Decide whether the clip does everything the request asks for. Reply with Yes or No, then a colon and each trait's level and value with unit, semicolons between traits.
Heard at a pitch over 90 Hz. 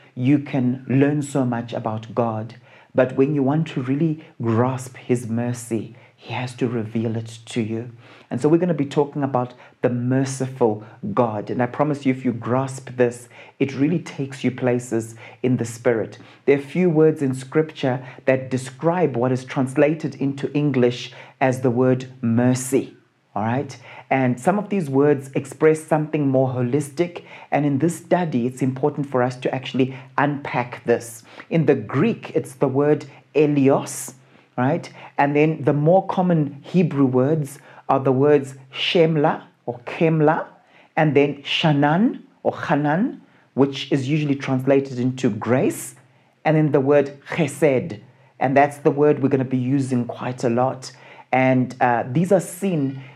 Yes: low, 135 Hz